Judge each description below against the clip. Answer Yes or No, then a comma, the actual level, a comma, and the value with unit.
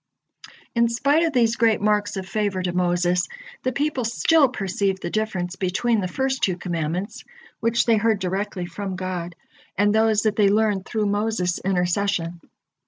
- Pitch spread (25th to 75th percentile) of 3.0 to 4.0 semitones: Yes, average, 3.6 semitones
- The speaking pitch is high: Yes, high, 205 Hz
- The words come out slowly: No, average, 165 wpm